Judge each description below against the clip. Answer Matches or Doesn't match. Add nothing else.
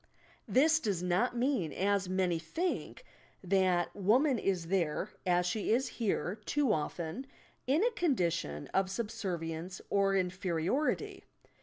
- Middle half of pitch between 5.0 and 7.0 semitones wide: Matches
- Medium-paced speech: Doesn't match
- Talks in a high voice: Matches